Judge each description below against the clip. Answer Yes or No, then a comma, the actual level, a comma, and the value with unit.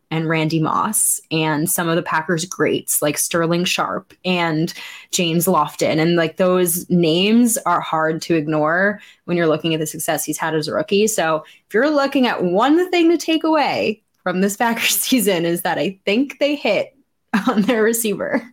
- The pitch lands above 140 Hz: Yes, medium, 185 Hz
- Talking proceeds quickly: No, average, 185 wpm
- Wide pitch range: Yes, wide, 6.2 semitones